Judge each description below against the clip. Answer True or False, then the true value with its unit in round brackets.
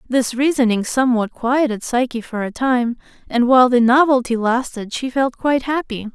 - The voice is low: False (250 Hz)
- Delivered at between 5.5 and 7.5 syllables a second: False (5.1 syllables/s)